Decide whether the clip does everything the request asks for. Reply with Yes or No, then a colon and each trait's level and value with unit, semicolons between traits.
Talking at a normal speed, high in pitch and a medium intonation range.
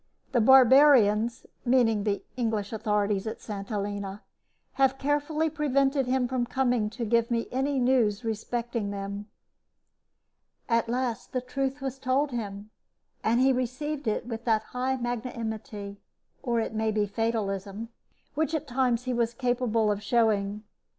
Yes: average, 145 wpm; high, 235 Hz; average, 3.5 semitones